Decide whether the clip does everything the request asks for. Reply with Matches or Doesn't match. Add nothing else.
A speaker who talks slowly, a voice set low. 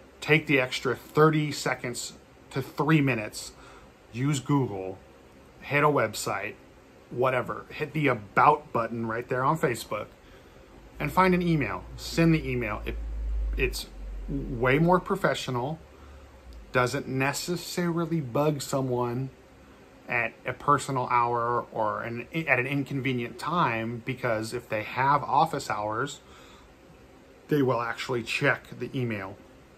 Matches